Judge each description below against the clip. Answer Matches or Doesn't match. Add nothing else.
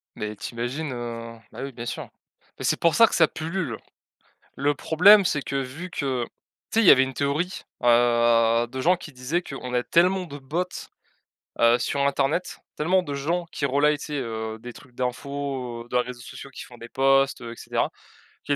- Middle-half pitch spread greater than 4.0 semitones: Matches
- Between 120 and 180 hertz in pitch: Matches